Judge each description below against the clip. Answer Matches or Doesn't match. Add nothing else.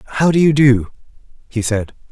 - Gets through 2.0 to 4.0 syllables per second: Doesn't match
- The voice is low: Matches